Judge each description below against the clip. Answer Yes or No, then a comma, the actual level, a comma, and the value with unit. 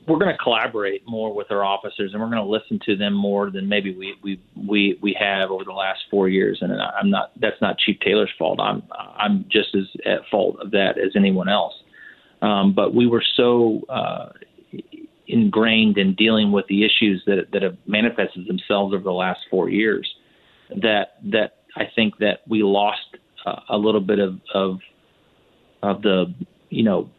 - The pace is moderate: Yes, average, 190 wpm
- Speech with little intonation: Yes, narrow, 2.0 semitones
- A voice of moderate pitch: No, low, 100 Hz